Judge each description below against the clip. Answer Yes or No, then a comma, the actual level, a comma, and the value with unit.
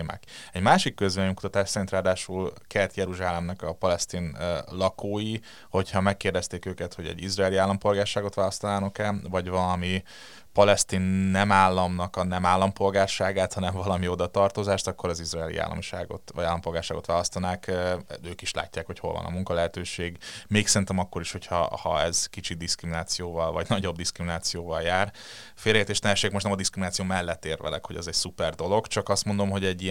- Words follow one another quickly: Yes, fast, 160 wpm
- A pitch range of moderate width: No, narrow, 2.2 semitones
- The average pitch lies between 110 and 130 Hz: No, very low, 95 Hz